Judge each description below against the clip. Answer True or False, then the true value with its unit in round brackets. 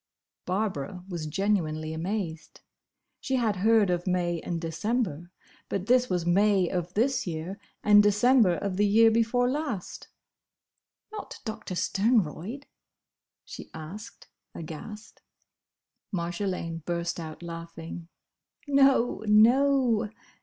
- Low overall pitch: False (195 Hz)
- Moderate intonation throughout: True (4.8 semitones)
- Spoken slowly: True (110 wpm)